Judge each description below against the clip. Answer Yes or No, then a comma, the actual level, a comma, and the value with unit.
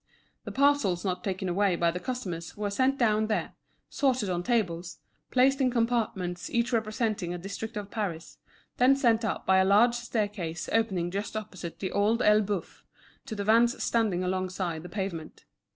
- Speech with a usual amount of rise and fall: Yes, average, 4.3 semitones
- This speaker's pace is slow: No, average, 170 wpm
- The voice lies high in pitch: Yes, high, 205 Hz